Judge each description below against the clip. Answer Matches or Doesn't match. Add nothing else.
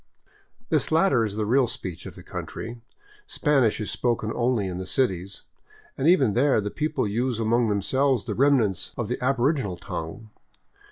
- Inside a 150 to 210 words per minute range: Matches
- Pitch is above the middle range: Doesn't match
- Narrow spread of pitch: Doesn't match